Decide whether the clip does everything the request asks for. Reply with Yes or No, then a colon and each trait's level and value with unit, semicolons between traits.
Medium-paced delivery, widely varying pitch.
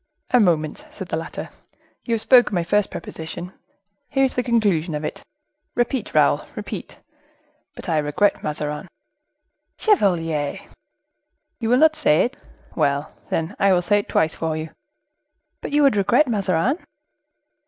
Yes: average, 145 wpm; wide, 7.3 semitones